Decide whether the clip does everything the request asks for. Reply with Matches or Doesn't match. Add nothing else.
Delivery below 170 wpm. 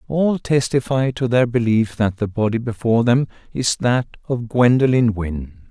Matches